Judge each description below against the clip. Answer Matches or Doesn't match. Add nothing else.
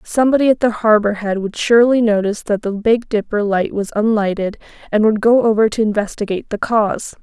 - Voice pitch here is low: Doesn't match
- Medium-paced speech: Matches